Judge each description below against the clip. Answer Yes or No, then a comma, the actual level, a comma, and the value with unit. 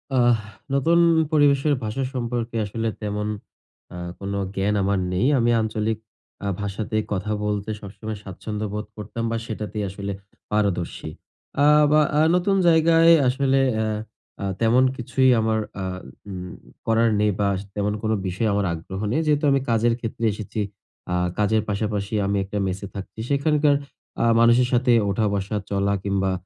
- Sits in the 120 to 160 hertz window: No, low, 110 Hz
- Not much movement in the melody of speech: No, average, 3.4 semitones